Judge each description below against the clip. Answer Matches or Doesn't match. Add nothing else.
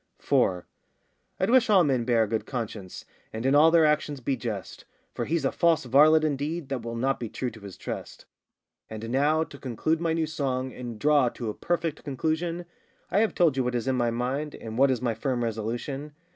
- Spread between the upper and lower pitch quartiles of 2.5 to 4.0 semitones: Doesn't match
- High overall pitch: Doesn't match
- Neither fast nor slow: Doesn't match